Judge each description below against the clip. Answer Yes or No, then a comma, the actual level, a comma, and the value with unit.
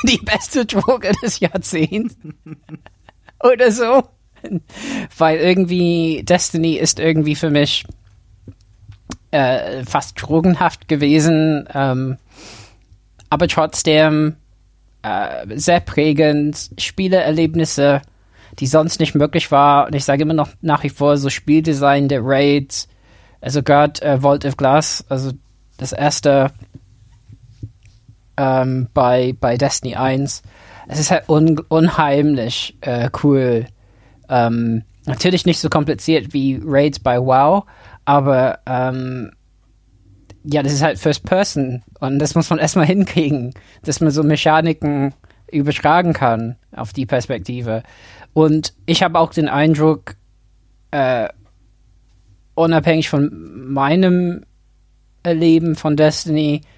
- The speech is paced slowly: Yes, slow, 115 wpm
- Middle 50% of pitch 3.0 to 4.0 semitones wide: No, average, 5.2 semitones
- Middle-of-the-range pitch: Yes, medium, 145 Hz